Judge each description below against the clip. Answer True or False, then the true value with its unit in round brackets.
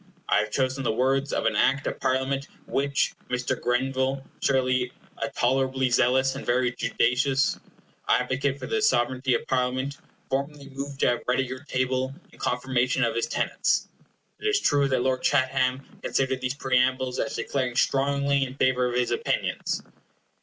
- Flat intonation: True (1.3 semitones)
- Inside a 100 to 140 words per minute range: False (165 wpm)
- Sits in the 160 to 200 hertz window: False (130 Hz)